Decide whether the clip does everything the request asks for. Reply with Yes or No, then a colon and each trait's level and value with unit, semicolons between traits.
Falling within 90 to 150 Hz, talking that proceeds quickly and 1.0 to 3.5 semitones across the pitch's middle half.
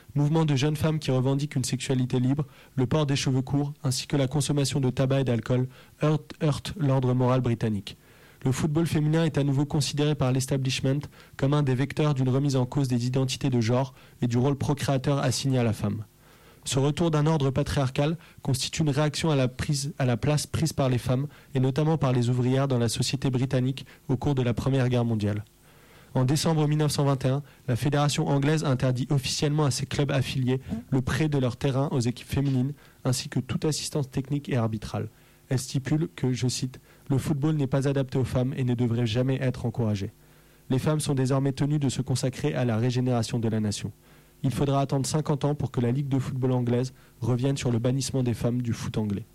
No: low, 135 Hz; average, 205 wpm; narrow, 2.5 semitones